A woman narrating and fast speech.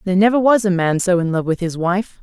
Yes: female; fast, 295 wpm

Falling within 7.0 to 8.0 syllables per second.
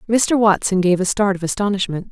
No: 5.7 syllables/s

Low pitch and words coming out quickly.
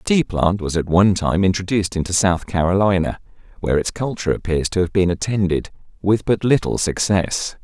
No: very low, 95 Hz; average, 180 wpm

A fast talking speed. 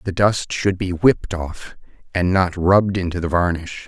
No: average, 185 wpm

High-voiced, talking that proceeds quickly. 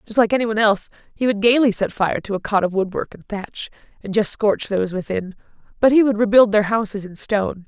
Yes: high, 210 Hz; fast, 235 wpm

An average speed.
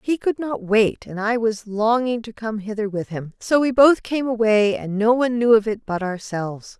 No: fast, 230 wpm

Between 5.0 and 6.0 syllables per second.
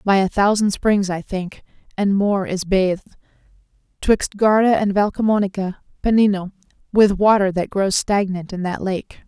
No: 4.8 syllables/s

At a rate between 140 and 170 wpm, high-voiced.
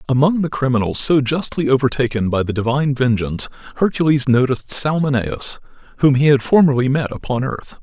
No: average, 155 wpm; low, 135 Hz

